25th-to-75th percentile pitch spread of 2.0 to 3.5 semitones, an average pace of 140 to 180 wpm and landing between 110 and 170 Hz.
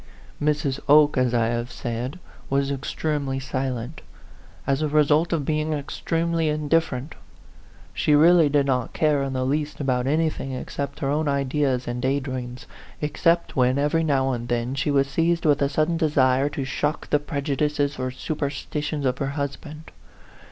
Yes: narrow, 2.5 semitones; average, 165 wpm; medium, 140 Hz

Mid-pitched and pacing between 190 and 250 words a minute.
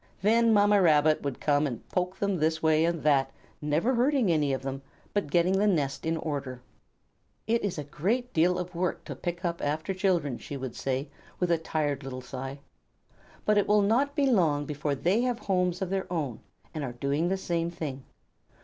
Yes: medium, 165 Hz; average, 200 wpm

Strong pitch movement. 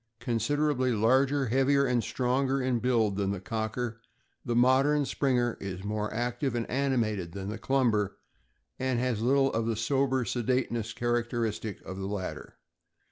No: average, 3.2 semitones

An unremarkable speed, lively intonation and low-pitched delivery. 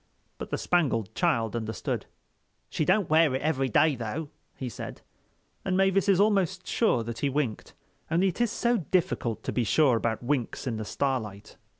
No: average, 180 wpm; wide, 7.7 semitones; medium, 145 Hz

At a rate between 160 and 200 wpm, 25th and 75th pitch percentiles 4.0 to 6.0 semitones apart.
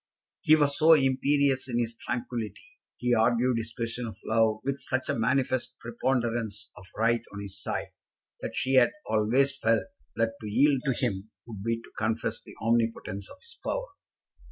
No: average, 175 wpm; average, 2.9 semitones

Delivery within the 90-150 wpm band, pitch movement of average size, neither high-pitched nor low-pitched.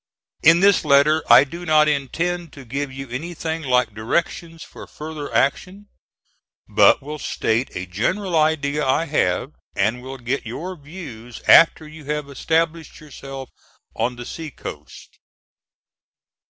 Yes: average, 140 wpm; average, 3.8 semitones; medium, 150 Hz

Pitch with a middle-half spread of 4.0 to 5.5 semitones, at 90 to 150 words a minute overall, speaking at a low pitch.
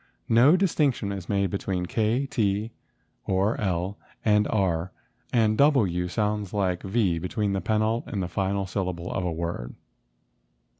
No: average, 3.2 semitones; average, 145 wpm; low, 100 Hz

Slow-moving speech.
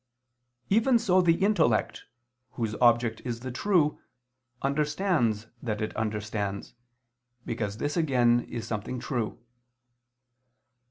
Yes: slow, 105 wpm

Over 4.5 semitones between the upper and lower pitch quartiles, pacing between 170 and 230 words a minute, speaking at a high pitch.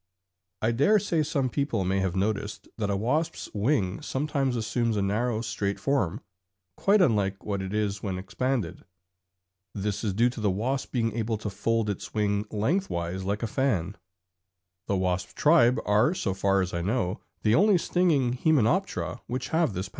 No: average, 5.2 semitones; average, 175 wpm; low, 110 Hz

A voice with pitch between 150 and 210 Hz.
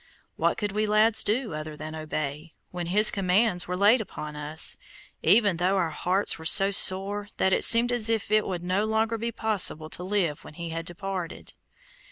Yes: high, 190 Hz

